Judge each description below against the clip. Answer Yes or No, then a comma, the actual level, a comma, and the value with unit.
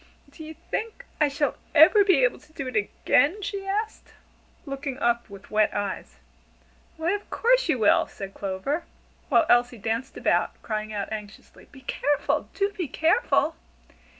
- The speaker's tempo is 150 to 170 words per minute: Yes, average, 160 wpm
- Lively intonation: Yes, wide, 8.2 semitones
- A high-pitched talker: Yes, very high, 280 Hz